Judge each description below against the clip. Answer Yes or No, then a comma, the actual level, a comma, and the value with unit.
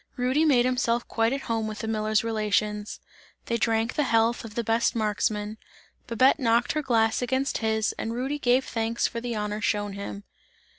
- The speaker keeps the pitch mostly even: Yes, narrow, 2.3 semitones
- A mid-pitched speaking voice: No, high, 230 Hz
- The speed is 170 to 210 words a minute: Yes, average, 185 wpm